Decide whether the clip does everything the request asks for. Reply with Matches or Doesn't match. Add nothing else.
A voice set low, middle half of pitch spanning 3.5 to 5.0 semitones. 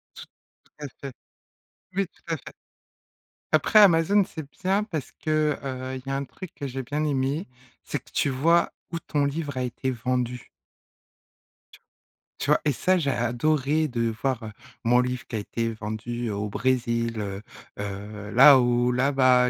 Matches